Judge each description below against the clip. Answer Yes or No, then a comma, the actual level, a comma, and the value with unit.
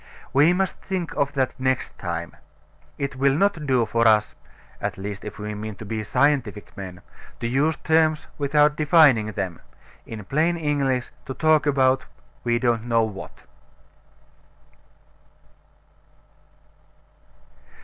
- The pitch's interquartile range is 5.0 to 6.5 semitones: Yes, wide, 5.5 semitones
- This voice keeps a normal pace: No, slow, 130 wpm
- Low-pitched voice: Yes, low, 130 Hz